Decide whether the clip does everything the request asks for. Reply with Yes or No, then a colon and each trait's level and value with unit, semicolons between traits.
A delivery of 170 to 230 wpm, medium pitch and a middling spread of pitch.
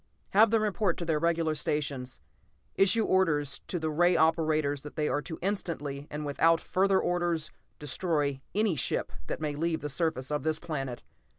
Yes: average, 175 wpm; medium, 160 Hz; average, 3.0 semitones